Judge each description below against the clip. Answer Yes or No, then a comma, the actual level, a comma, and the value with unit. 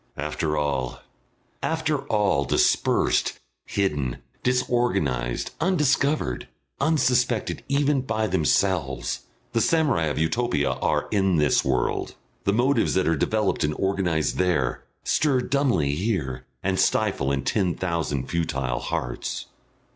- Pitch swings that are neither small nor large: No, wide, 9.0 semitones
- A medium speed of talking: No, slow, 115 wpm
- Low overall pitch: Yes, very low, 95 Hz